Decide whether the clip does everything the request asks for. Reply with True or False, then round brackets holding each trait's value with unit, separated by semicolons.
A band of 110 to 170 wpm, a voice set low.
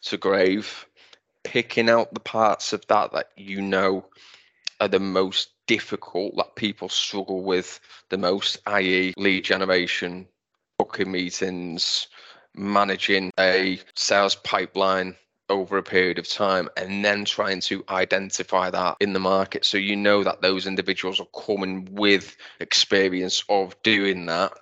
True (140 wpm; 95 Hz)